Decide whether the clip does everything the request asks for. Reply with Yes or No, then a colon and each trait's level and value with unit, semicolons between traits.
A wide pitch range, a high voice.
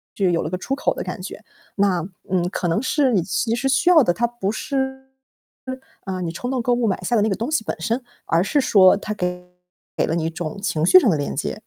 Yes: wide, 5.7 semitones; high, 205 Hz